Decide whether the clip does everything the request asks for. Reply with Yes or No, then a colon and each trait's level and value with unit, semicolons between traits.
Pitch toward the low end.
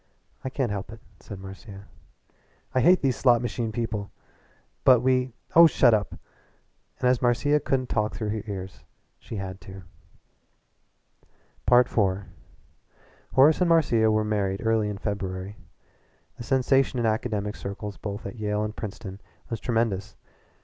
Yes: low, 110 Hz